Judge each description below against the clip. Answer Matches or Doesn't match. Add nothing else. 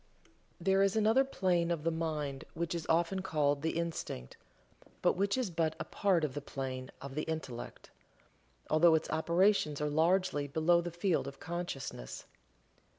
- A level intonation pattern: Doesn't match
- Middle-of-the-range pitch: Matches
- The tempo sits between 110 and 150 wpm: Doesn't match